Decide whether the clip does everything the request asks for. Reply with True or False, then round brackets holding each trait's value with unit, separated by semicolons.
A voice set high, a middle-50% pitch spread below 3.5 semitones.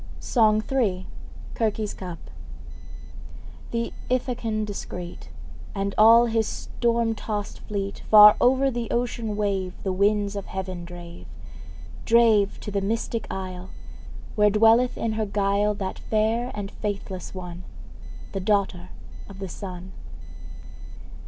True (210 Hz; 2.8 semitones)